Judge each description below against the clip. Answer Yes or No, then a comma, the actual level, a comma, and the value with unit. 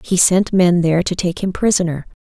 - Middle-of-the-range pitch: Yes, medium, 180 Hz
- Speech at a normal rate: No, fast, 215 wpm